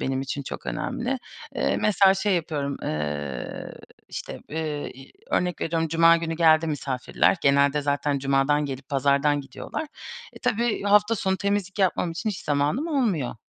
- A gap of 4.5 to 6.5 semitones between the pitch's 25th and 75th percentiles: Yes, wide, 5.5 semitones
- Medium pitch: Yes, medium, 155 Hz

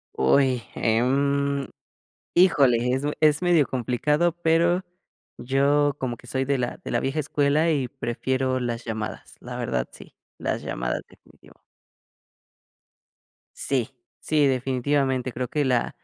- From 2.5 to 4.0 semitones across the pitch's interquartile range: Yes, average, 2.8 semitones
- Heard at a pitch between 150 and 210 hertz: No, low, 135 Hz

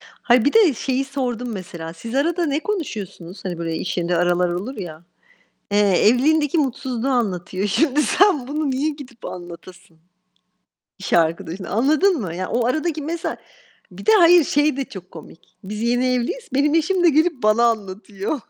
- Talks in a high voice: Yes, high, 245 Hz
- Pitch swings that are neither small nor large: No, wide, 8.1 semitones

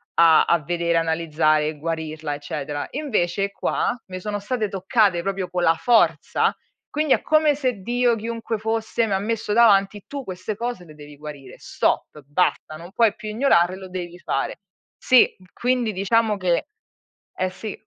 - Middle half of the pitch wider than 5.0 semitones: Yes, wide, 5.4 semitones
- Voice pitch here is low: No, high, 190 Hz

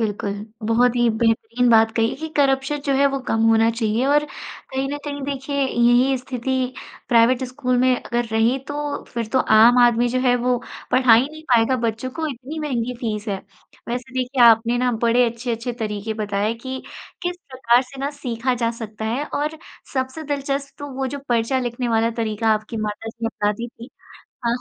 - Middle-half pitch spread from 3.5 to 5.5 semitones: No, average, 2.7 semitones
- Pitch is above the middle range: Yes, high, 245 Hz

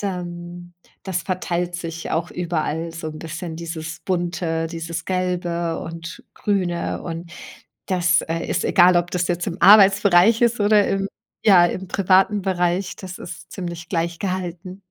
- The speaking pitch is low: No, medium, 175 Hz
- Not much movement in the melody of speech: Yes, narrow, 1.8 semitones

